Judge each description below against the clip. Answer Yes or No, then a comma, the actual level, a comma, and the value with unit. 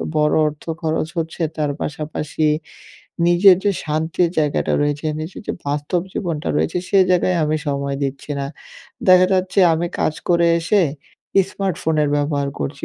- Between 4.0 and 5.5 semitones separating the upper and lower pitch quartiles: No, average, 3.0 semitones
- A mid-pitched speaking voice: Yes, medium, 155 Hz